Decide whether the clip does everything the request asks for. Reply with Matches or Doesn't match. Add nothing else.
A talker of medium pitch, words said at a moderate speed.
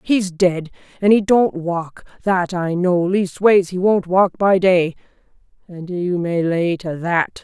Matches